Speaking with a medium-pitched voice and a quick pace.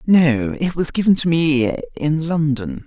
No: medium, 150 Hz; average, 165 wpm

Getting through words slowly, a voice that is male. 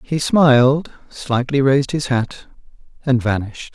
Yes: slow, 130 wpm; male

